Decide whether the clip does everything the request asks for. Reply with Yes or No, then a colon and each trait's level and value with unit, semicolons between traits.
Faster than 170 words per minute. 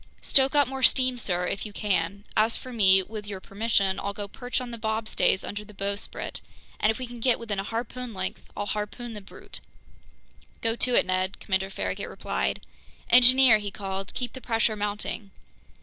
Yes: average, 190 wpm